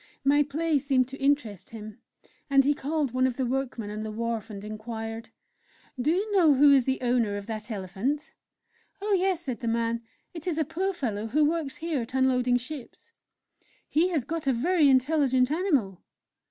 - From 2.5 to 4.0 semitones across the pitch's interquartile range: No, average, 4.8 semitones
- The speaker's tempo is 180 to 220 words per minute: Yes, average, 185 wpm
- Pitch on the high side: Yes, very high, 265 Hz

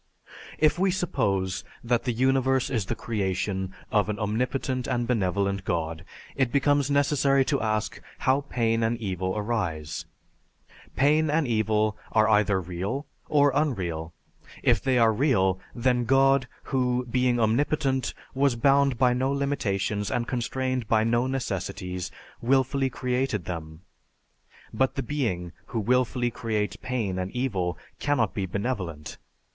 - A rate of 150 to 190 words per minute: No, slow, 135 wpm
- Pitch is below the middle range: Yes, low, 120 Hz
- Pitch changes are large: No, average, 5.0 semitones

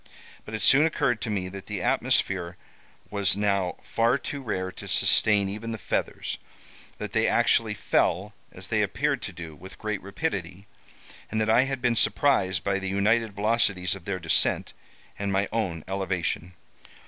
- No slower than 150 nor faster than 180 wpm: Yes, average, 170 wpm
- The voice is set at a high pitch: No, low, 100 Hz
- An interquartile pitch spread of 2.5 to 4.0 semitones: Yes, average, 3.1 semitones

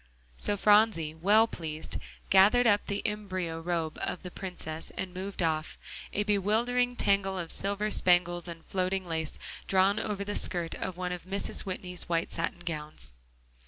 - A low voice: No, medium, 185 Hz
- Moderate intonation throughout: Yes, average, 3.3 semitones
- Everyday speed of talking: Yes, average, 160 wpm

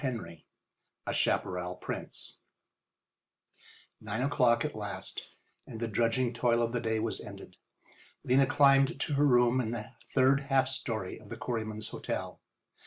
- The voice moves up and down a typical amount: Yes, average, 3.2 semitones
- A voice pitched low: Yes, low, 120 Hz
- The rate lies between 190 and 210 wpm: No, average, 145 wpm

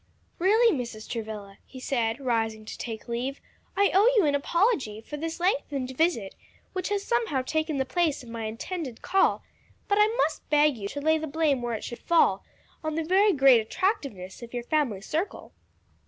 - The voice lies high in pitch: Yes, very high, 280 Hz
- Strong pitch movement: Yes, wide, 6.6 semitones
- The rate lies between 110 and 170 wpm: No, average, 185 wpm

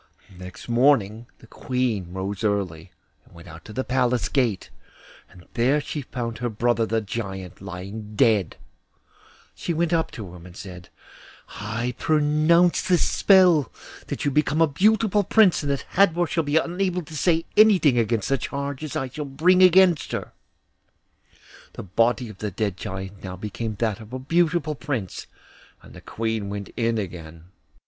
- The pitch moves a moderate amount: No, wide, 7.4 semitones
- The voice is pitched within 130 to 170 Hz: No, low, 120 Hz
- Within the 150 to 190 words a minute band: Yes, average, 165 wpm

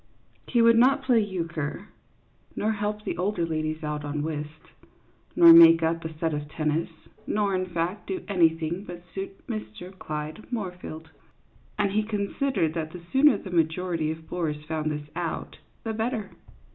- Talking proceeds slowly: No, average, 165 wpm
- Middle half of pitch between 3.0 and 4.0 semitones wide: No, average, 4.7 semitones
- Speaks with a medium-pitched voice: Yes, medium, 170 Hz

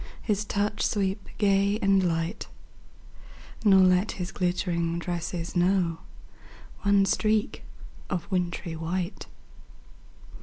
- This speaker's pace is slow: Yes, slow, 100 wpm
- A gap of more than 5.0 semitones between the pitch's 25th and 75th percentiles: No, narrow, 2.5 semitones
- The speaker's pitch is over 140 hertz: Yes, medium, 185 Hz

